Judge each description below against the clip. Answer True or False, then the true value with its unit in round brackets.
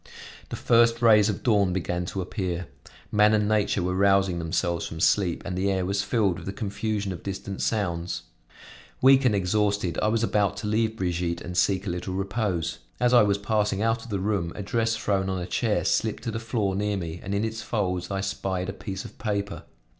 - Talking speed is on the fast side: True (215 wpm)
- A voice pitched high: False (100 Hz)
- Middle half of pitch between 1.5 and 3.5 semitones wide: True (2.8 semitones)